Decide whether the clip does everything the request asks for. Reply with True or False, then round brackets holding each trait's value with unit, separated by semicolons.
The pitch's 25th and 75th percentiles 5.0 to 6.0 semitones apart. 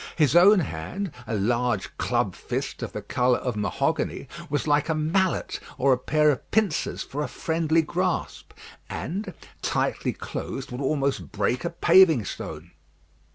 True (5.4 semitones)